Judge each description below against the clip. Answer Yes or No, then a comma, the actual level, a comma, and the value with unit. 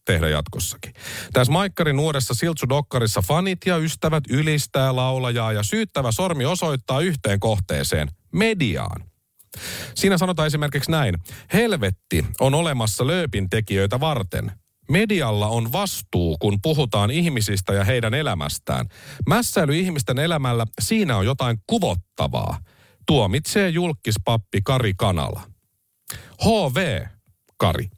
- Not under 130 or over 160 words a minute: No, average, 105 wpm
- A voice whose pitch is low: Yes, low, 130 Hz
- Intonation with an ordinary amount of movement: No, wide, 7.0 semitones